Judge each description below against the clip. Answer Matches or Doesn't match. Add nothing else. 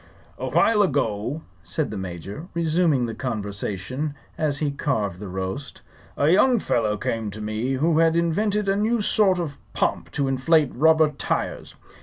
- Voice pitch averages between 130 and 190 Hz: Matches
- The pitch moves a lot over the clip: Matches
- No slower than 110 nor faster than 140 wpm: Doesn't match